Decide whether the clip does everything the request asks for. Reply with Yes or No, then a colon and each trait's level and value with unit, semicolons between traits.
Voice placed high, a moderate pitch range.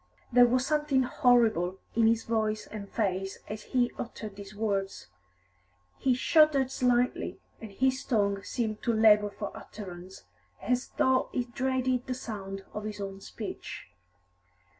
Yes: high, 225 Hz; average, 3.8 semitones